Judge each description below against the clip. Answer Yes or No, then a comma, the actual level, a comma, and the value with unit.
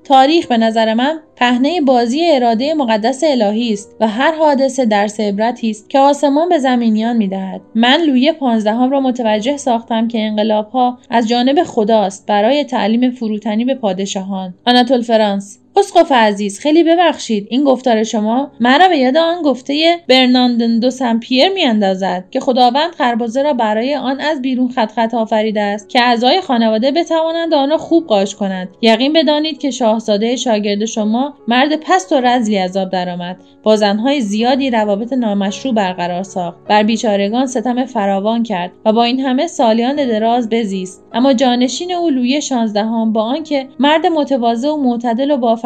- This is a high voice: Yes, high, 245 Hz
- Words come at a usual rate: No, fast, 165 wpm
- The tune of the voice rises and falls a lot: No, average, 4.2 semitones